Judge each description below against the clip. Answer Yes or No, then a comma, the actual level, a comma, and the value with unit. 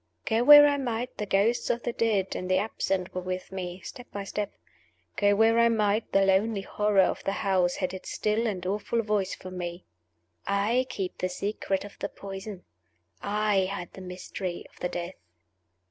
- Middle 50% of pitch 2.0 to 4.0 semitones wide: Yes, average, 2.9 semitones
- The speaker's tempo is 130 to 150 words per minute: No, average, 190 wpm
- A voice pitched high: Yes, high, 200 Hz